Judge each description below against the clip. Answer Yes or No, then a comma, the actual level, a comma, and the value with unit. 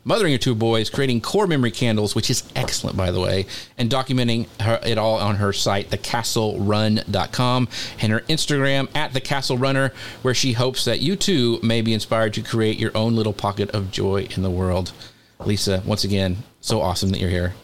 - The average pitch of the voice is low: Yes, low, 115 Hz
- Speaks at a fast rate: No, average, 190 wpm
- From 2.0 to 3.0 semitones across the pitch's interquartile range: No, average, 3.8 semitones